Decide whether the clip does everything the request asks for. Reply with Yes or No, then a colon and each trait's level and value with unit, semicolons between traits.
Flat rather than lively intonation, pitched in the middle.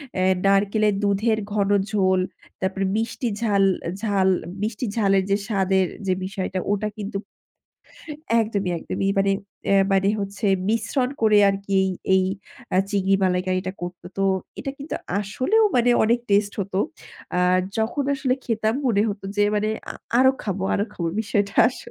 No: narrow, 2.3 semitones; high, 200 Hz